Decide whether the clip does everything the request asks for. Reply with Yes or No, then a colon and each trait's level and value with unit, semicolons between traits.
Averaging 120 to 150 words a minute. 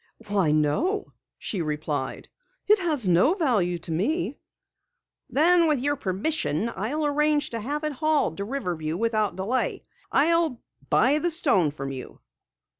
Yes: average, 140 wpm